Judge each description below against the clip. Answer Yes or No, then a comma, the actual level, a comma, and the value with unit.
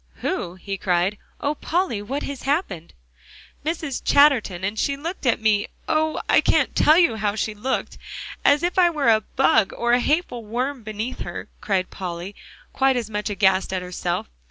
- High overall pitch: Yes, high, 230 Hz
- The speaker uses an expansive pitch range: Yes, wide, 6.2 semitones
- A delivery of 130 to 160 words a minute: No, average, 180 wpm